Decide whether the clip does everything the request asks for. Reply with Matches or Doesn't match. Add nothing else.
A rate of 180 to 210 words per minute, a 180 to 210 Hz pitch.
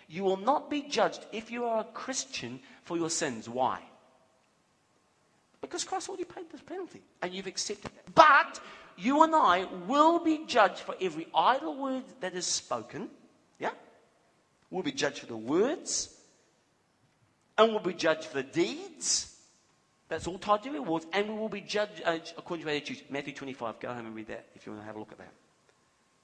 Matches